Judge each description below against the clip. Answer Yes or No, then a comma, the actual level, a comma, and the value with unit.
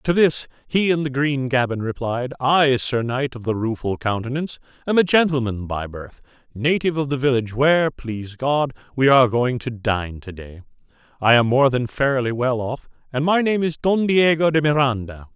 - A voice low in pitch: Yes, low, 130 Hz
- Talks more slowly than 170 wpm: No, average, 190 wpm